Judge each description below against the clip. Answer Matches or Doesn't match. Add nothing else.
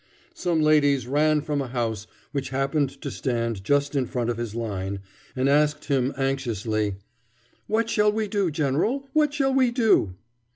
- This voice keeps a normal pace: Matches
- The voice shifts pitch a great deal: Matches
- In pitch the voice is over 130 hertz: Matches